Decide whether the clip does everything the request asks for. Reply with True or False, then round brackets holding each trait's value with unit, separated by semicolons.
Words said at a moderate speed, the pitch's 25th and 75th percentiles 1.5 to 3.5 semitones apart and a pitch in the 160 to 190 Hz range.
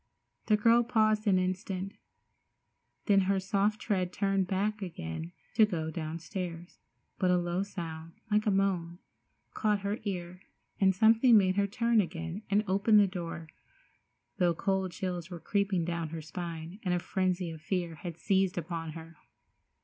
True (155 wpm; 2.9 semitones; 185 Hz)